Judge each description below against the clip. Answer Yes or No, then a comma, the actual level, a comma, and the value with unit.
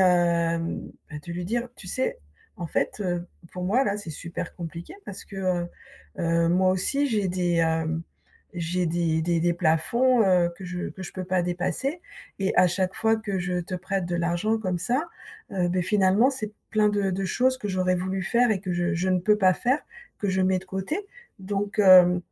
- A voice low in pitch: No, medium, 185 Hz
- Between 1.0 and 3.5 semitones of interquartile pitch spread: Yes, average, 2.8 semitones